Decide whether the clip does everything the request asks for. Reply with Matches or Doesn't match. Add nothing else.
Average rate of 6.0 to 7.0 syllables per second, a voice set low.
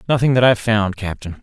Matches